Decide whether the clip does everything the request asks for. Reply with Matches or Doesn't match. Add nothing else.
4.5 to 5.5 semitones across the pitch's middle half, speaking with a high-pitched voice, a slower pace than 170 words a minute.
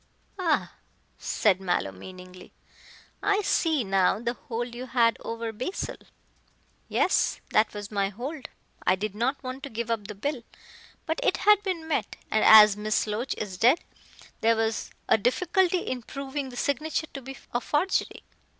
Matches